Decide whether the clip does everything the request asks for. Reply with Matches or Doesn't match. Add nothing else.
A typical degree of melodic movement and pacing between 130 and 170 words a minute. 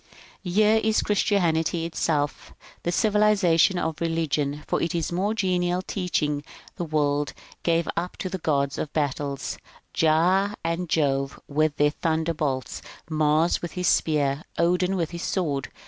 Matches